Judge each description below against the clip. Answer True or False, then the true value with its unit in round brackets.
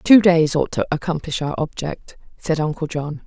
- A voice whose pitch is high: False (160 Hz)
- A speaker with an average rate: True (185 wpm)